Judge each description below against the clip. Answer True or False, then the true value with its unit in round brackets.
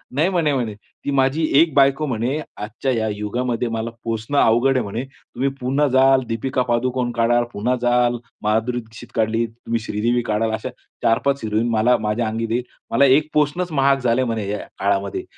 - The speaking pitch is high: False (120 Hz)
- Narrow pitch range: False (3.2 semitones)